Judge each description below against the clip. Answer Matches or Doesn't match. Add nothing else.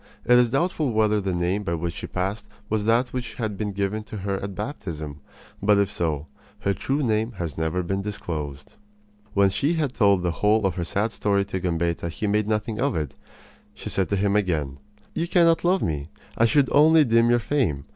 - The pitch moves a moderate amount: Matches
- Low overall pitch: Matches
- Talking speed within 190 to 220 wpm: Matches